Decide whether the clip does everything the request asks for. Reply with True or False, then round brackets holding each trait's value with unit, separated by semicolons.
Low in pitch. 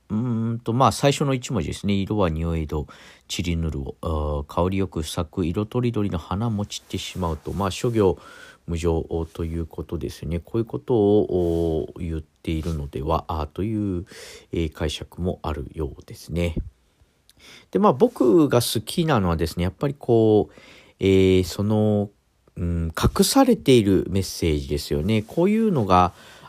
True (95 Hz)